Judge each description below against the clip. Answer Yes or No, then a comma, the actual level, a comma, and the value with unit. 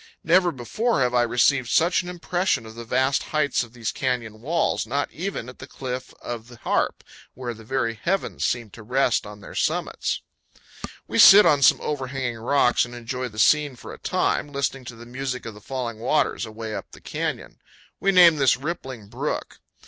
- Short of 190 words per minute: No, average, 195 wpm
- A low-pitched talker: Yes, low, 125 Hz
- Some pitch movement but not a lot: Yes, average, 3.6 semitones